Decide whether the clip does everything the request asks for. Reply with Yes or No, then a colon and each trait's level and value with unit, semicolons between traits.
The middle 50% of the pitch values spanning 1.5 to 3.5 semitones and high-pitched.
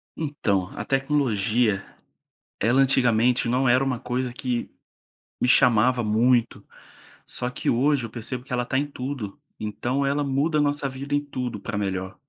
No: average, 2.8 semitones; low, 125 Hz